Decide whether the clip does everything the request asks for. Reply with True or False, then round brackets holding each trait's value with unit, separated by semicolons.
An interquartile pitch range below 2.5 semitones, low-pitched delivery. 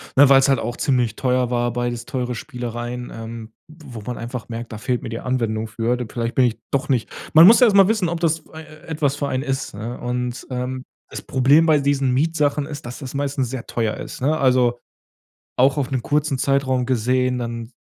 False (2.8 semitones; 130 Hz)